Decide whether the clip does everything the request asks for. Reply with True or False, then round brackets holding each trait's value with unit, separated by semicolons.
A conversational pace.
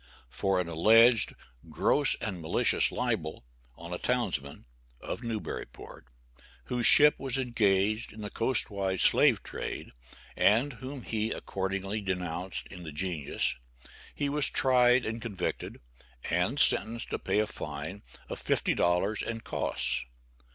False (130 wpm)